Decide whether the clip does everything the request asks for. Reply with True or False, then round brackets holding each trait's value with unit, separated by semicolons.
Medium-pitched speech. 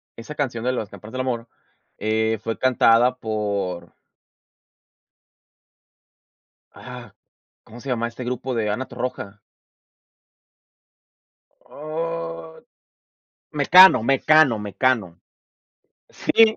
False (115 Hz)